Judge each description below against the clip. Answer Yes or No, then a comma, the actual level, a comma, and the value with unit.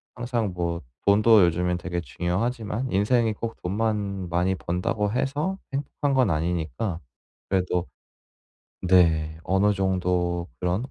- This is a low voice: Yes, very low, 95 Hz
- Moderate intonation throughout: Yes, average, 4.3 semitones